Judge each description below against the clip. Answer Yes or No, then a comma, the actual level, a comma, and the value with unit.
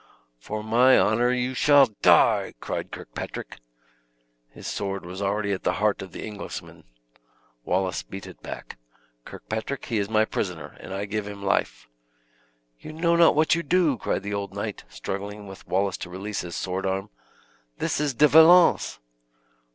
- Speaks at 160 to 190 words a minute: Yes, average, 165 wpm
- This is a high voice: No, low, 105 Hz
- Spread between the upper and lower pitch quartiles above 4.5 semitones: Yes, average, 4.9 semitones